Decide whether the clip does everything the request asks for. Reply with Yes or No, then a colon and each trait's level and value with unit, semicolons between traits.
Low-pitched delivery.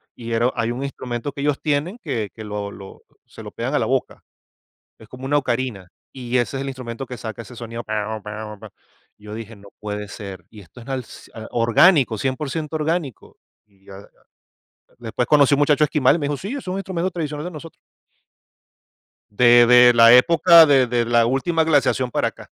Yes: low, 125 Hz